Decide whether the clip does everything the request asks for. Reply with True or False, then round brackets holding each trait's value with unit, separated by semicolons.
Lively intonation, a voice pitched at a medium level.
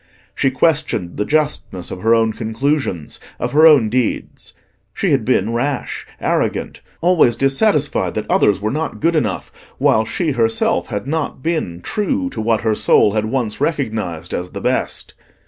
False (5.8 semitones; 120 Hz)